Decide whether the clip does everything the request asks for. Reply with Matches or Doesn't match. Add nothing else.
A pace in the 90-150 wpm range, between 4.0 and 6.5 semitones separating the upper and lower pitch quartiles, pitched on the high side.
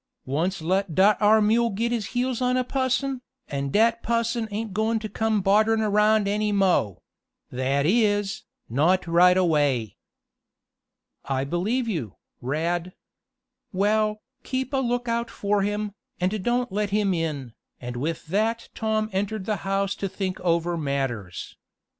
Matches